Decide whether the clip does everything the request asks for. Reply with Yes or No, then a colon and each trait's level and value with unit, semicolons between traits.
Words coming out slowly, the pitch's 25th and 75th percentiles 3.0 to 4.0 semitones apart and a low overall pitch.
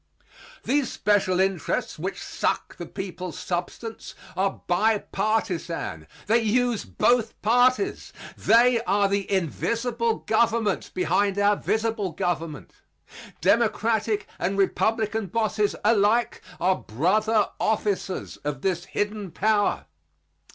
No: slow, 105 wpm; average, 3.3 semitones; high, 210 Hz